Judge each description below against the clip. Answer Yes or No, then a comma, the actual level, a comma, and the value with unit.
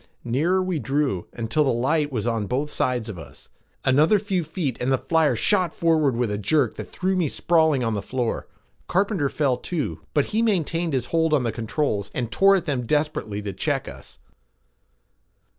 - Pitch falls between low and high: Yes, medium, 145 Hz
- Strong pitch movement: Yes, wide, 5.7 semitones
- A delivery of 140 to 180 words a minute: No, average, 190 wpm